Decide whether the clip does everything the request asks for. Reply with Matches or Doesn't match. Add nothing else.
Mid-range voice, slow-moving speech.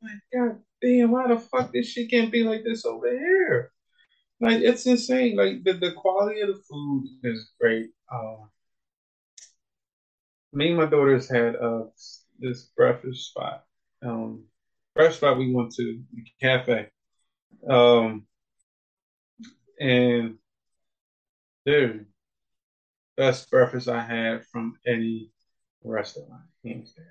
Doesn't match